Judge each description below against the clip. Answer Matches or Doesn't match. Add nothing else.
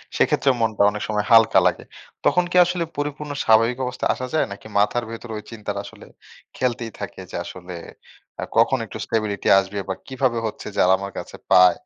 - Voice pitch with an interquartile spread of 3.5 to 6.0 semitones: Matches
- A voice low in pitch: Matches